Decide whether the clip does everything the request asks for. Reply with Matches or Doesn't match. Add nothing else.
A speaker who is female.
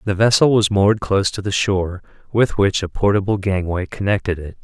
Doesn't match